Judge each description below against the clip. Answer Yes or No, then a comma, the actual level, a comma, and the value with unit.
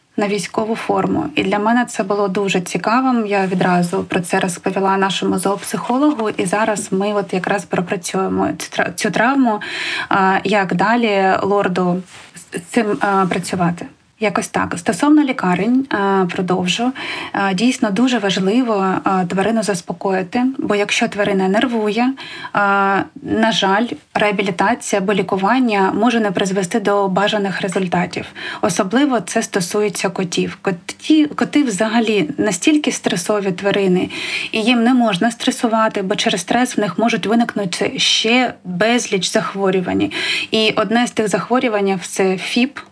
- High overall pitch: Yes, high, 210 Hz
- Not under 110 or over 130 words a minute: Yes, average, 125 wpm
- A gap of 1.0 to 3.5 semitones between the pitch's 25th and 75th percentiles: Yes, average, 3.2 semitones